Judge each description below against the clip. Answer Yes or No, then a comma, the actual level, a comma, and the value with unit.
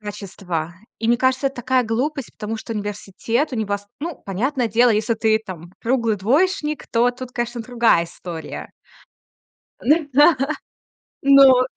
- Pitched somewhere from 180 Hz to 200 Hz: No, high, 235 Hz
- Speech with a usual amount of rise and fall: Yes, average, 4.0 semitones